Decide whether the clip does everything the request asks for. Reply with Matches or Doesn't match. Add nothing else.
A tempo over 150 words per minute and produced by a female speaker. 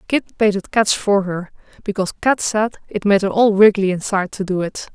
Matches